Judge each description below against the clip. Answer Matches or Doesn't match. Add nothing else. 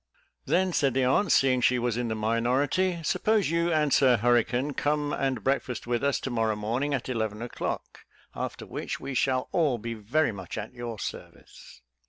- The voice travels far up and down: Doesn't match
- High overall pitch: Doesn't match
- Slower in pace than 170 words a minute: Doesn't match